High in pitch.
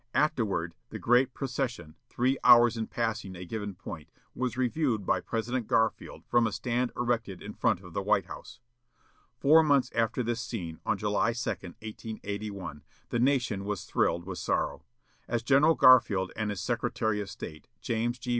No: low, 115 Hz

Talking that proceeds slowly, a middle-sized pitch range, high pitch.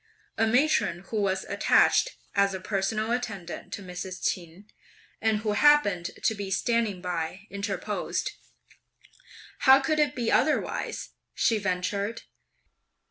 Yes: slow, 125 wpm; average, 3.5 semitones; high, 205 Hz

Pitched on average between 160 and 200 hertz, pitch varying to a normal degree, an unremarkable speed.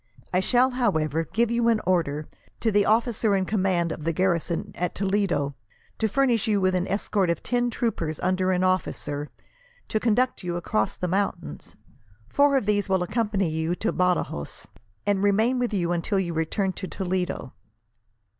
Yes: high, 190 Hz; average, 4.1 semitones; average, 170 wpm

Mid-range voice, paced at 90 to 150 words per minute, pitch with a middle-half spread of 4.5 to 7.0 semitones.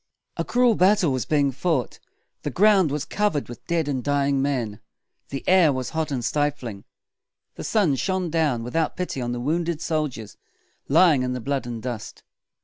No: medium, 145 Hz; average, 175 wpm; average, 4.9 semitones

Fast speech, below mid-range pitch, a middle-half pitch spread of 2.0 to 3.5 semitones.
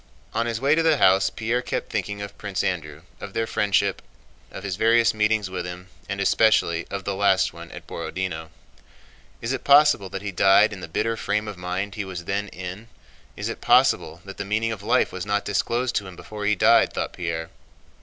Yes: fast, 210 wpm; low, 100 Hz; average, 2.9 semitones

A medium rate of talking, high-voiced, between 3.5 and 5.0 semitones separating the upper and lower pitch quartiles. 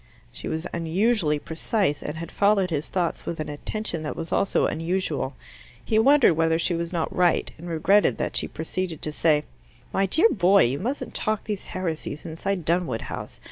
No: average, 180 wpm; medium, 170 Hz; average, 3.8 semitones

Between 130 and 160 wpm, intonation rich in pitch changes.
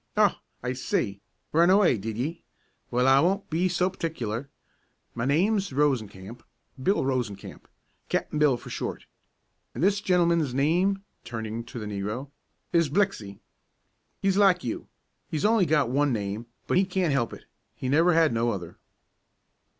Yes: average, 150 wpm; wide, 7.4 semitones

